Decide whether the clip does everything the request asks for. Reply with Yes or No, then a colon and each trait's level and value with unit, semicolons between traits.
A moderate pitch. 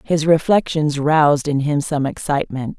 Yes: medium, 150 Hz